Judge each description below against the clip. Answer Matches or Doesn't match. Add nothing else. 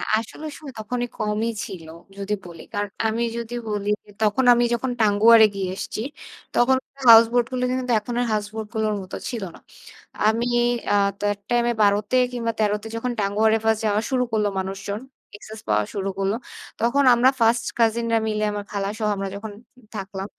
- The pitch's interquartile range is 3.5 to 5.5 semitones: Doesn't match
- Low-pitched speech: Doesn't match